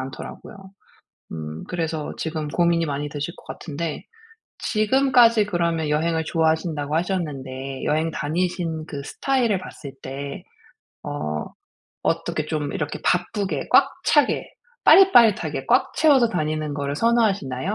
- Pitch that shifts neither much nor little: Yes, average, 4.6 semitones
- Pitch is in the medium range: Yes, medium, 160 Hz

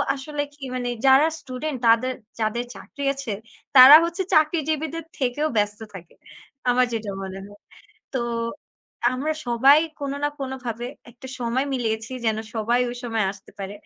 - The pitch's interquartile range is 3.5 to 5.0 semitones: Yes, average, 4.0 semitones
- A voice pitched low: No, very high, 255 Hz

